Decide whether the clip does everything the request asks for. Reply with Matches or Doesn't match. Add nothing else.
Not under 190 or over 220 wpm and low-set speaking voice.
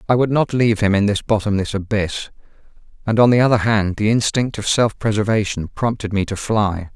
Matches